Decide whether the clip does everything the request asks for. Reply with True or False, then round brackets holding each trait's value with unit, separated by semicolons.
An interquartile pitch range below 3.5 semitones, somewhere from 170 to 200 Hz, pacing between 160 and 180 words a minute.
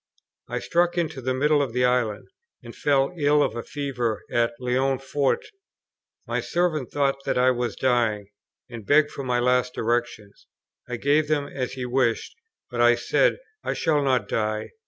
False (3.1 semitones; 130 Hz; 170 wpm)